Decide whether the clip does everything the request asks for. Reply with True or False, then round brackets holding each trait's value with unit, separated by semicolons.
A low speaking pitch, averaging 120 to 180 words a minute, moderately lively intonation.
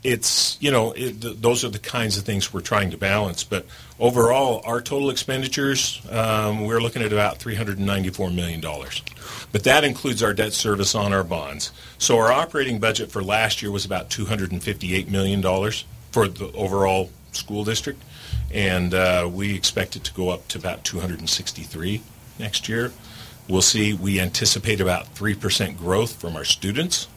True (105 Hz; 170 wpm; 3.2 semitones)